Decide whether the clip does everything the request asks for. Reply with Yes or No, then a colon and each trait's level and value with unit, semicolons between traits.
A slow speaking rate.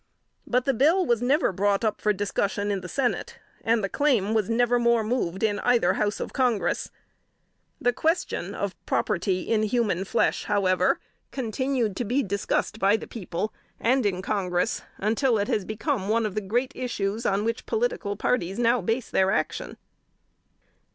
No: average, 170 wpm